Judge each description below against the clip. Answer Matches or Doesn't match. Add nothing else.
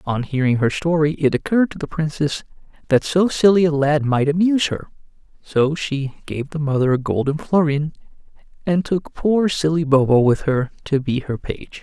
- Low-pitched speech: Doesn't match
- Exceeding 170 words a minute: Matches